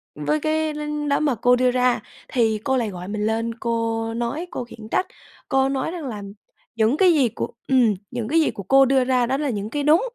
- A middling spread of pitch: Yes, average, 4.3 semitones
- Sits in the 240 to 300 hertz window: Yes, very high, 250 Hz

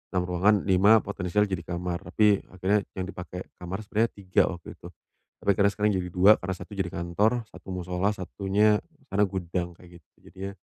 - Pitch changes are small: Yes, narrow, 2.2 semitones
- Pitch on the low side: Yes, very low, 95 Hz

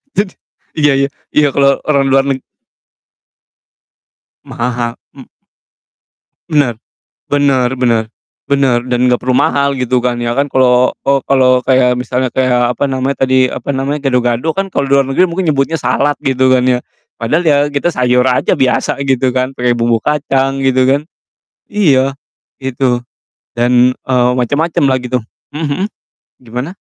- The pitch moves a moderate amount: No, narrow, 2.1 semitones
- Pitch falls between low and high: No, low, 130 Hz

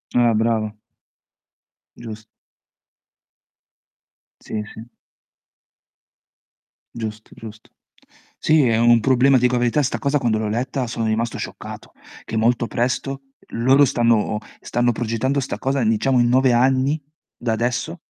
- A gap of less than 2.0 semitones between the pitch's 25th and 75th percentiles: No, narrow, 2.6 semitones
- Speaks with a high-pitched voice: No, low, 120 Hz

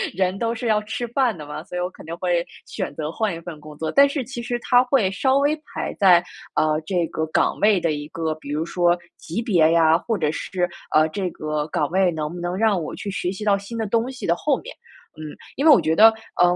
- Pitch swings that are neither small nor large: No, wide, 5.9 semitones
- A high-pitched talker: No, medium, 180 Hz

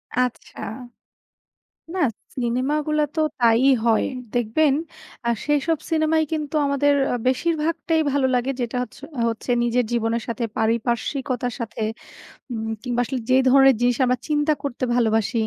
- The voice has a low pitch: No, very high, 250 Hz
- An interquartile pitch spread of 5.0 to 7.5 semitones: No, average, 3.8 semitones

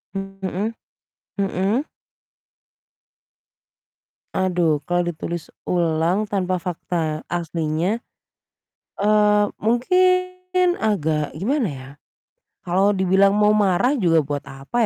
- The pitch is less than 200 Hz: Yes, high, 190 Hz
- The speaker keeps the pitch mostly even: No, average, 4.3 semitones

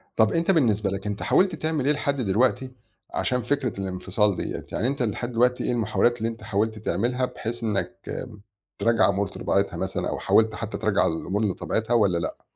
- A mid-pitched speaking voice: No, low, 115 Hz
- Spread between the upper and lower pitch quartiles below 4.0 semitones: Yes, average, 3.6 semitones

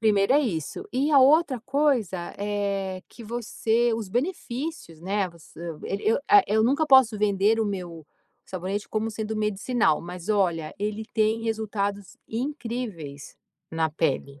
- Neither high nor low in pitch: No, high, 210 Hz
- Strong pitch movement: No, average, 4.4 semitones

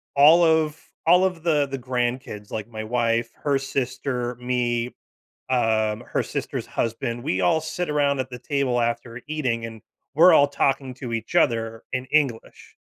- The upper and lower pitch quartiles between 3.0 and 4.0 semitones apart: Yes, average, 3.6 semitones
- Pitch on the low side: Yes, low, 125 Hz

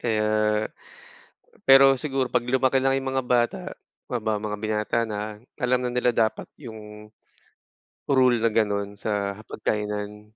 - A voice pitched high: No, low, 110 Hz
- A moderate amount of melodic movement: Yes, average, 3.0 semitones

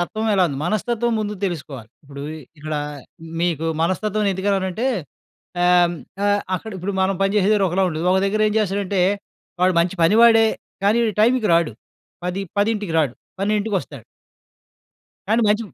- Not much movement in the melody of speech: No, average, 3.5 semitones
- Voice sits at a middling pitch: No, high, 195 Hz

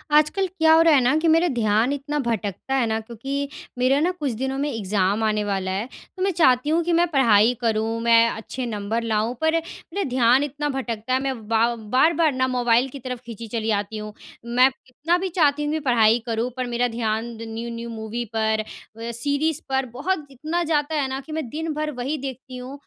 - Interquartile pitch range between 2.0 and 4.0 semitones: No, average, 4.7 semitones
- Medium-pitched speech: No, very high, 250 Hz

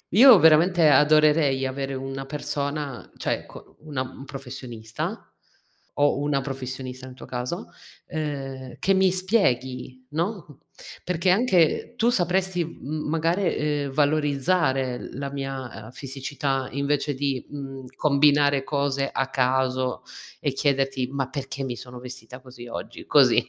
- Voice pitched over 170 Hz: No, medium, 140 Hz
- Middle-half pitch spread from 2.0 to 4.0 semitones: Yes, average, 2.7 semitones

